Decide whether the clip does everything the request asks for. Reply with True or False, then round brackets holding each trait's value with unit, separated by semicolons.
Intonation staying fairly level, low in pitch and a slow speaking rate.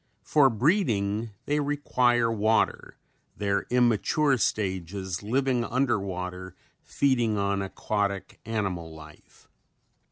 False (4.3 semitones; 110 Hz; 95 wpm)